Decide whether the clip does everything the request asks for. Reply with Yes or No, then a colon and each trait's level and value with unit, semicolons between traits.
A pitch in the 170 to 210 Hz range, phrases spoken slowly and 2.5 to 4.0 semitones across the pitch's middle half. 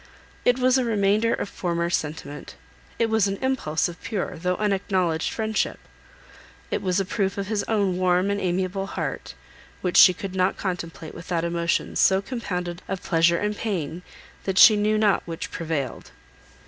No: high, 190 Hz; average, 165 wpm; average, 3.3 semitones